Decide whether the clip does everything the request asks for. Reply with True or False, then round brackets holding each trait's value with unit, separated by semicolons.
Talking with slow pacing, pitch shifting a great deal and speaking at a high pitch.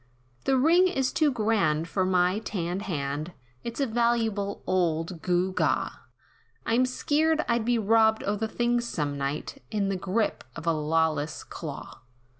False (155 wpm; 6.2 semitones; 200 Hz)